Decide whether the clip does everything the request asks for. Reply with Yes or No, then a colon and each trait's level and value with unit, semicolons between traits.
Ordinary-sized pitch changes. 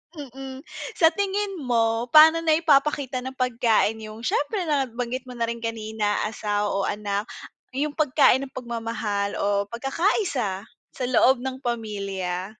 Yes: average, 4.7 semitones